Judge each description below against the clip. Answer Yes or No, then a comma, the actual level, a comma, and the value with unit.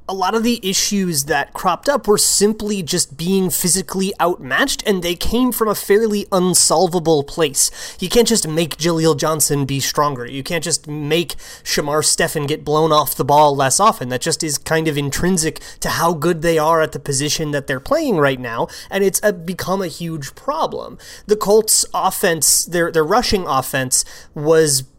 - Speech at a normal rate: Yes, average, 185 wpm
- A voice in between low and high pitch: Yes, medium, 165 Hz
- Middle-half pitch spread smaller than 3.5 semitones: No, average, 4.2 semitones